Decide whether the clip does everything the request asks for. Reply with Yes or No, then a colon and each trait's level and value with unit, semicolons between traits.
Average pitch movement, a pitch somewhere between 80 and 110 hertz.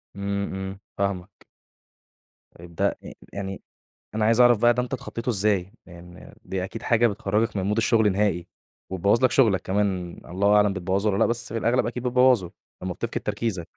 Yes: average, 3.4 semitones; low, 100 Hz